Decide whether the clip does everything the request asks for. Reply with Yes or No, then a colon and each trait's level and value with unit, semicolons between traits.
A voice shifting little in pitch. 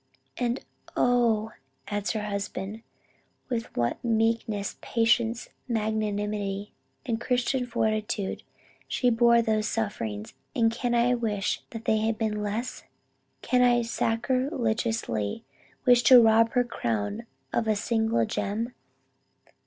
Yes: narrow, 2.2 semitones